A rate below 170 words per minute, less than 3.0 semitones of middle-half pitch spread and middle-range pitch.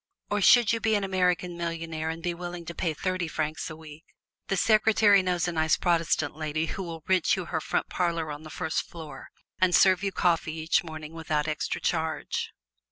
No: average, 200 wpm; narrow, 2.5 semitones; medium, 170 Hz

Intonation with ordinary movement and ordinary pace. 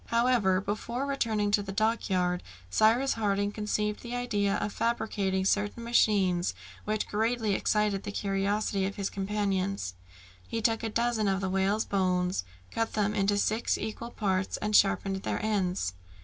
No: narrow, 2.3 semitones; average, 150 wpm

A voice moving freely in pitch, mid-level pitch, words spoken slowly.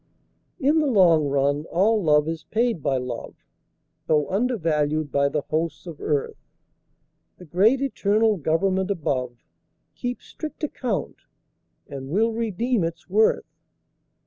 Yes: wide, 6.8 semitones; medium, 170 Hz; slow, 125 wpm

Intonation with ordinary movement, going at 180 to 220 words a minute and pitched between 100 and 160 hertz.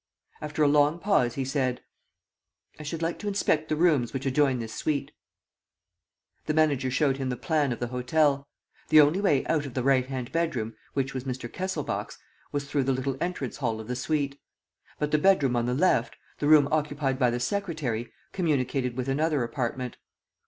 Yes: average, 3.3 semitones; average, 190 wpm; medium, 140 Hz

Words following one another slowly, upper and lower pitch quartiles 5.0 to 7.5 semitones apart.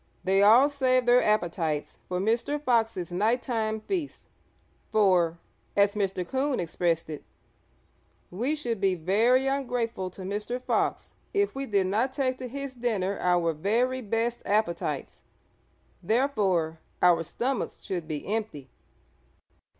Yes: slow, 130 wpm; wide, 5.6 semitones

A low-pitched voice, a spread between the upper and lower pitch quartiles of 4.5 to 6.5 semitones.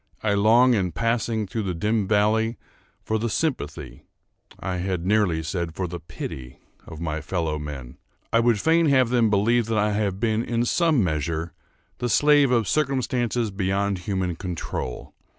Yes: low, 105 Hz; average, 4.9 semitones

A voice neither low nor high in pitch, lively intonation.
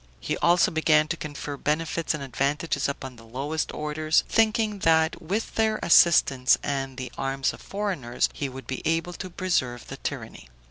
No: medium, 155 Hz; average, 4.3 semitones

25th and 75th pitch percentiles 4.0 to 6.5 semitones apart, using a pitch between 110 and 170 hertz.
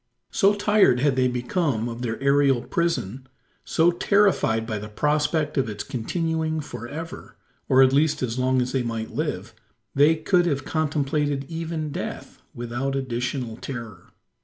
Yes: average, 4.6 semitones; low, 135 Hz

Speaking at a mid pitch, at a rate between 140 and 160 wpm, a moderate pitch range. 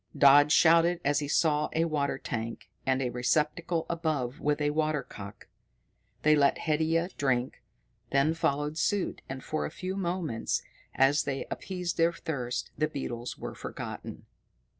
Yes: medium, 150 Hz; average, 155 wpm; average, 3.3 semitones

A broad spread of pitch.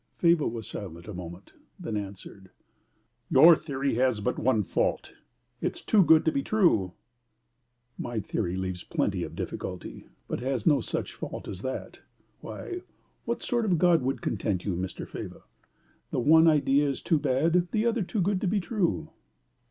Yes: wide, 8.8 semitones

